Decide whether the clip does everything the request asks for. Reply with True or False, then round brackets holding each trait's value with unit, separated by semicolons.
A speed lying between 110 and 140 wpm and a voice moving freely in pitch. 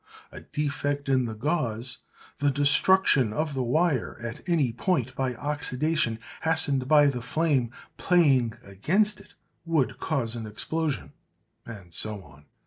False (135 wpm; 4.9 semitones)